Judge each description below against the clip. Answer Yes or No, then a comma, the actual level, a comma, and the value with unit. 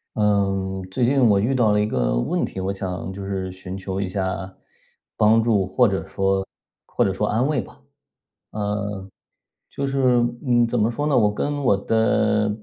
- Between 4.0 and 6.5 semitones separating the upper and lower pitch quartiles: No, average, 3.4 semitones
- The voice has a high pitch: No, low, 105 Hz